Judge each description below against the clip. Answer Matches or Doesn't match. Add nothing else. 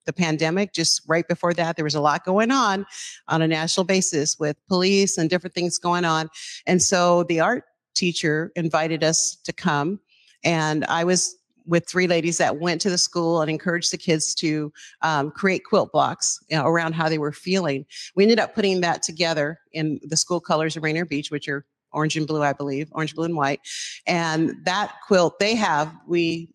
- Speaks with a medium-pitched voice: Matches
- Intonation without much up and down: Matches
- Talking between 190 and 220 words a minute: Matches